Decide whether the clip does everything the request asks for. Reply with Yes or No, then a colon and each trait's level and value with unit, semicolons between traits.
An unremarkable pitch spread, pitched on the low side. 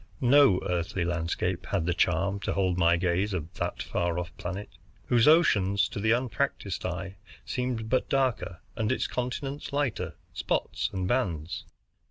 No: wide, 5.8 semitones; very low, 95 Hz